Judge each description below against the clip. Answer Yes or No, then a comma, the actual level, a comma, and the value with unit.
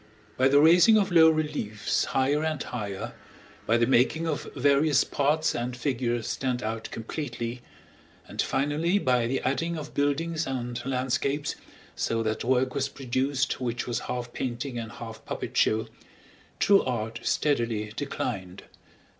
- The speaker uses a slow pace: No, average, 145 wpm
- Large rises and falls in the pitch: No, average, 3.7 semitones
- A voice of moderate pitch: No, low, 130 Hz